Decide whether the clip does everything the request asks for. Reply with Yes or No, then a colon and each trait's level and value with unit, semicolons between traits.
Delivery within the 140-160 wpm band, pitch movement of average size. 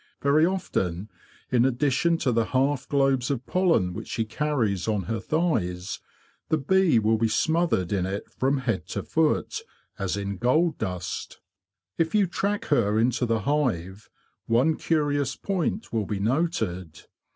No: average, 150 wpm; wide, 7.1 semitones